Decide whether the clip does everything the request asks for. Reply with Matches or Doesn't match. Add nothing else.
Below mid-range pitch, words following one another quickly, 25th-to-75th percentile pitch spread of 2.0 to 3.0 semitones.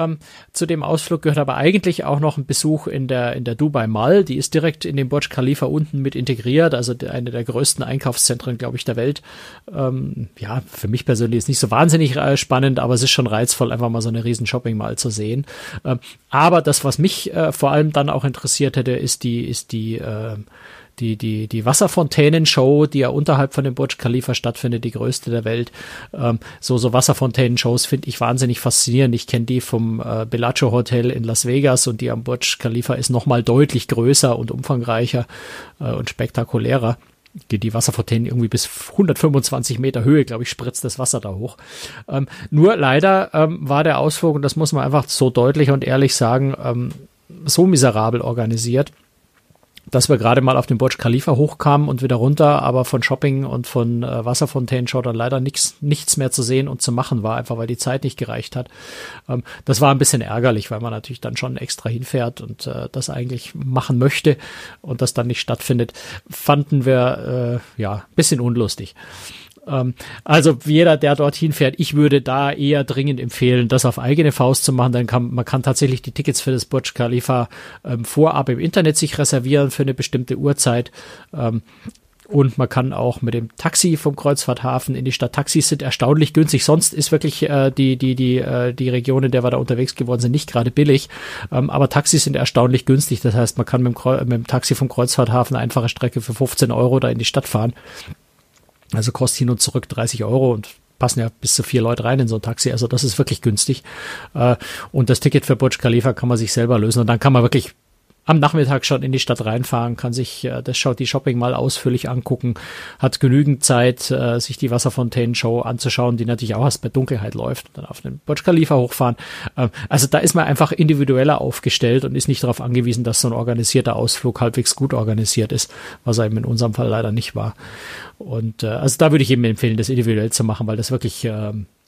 Matches